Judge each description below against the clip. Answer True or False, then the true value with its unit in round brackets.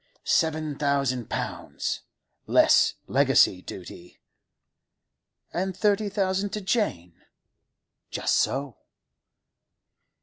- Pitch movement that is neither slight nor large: False (7.2 semitones)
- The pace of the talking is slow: True (70 wpm)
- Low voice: False (155 Hz)